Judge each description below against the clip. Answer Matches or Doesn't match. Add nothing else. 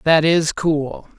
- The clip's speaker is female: Doesn't match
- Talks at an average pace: Matches